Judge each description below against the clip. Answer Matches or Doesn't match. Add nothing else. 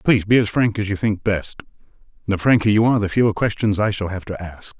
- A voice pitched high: Doesn't match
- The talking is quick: Matches